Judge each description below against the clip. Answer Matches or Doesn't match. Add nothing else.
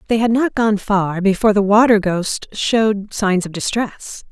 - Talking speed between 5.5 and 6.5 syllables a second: Doesn't match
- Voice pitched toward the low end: Doesn't match